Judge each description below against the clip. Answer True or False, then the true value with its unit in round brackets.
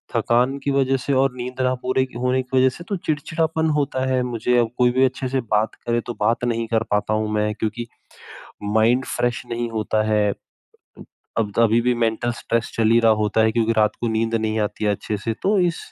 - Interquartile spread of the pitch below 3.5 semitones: True (2.8 semitones)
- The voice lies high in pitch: False (120 Hz)